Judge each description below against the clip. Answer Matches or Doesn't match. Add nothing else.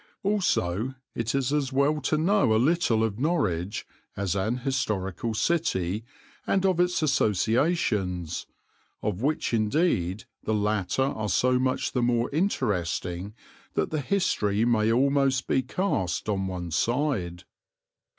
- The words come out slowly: Matches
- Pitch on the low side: Matches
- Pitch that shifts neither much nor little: Doesn't match